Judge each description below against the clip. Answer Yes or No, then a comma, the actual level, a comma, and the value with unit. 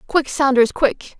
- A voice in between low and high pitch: No, very high, 265 Hz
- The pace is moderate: Yes, average, 150 wpm